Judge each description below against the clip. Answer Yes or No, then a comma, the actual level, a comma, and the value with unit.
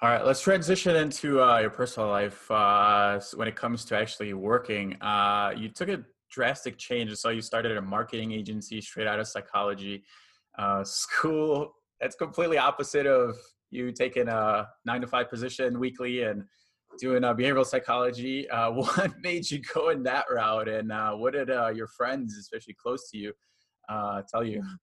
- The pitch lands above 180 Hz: No, low, 115 Hz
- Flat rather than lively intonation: No, average, 3.3 semitones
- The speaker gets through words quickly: No, average, 180 wpm